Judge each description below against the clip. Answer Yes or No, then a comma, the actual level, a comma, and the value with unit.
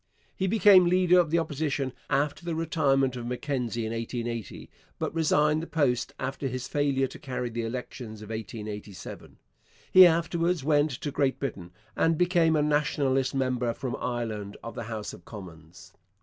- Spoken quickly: No, average, 165 wpm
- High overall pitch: No, low, 135 Hz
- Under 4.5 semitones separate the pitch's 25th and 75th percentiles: No, average, 5.2 semitones